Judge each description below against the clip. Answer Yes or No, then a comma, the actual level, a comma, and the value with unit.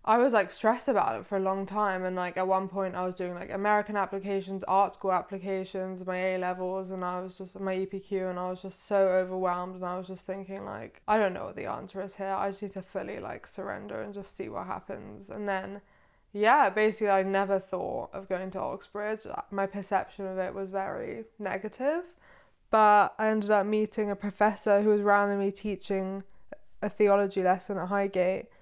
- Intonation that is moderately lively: No, narrow, 1.6 semitones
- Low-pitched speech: No, high, 195 Hz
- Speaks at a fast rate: Yes, fast, 210 wpm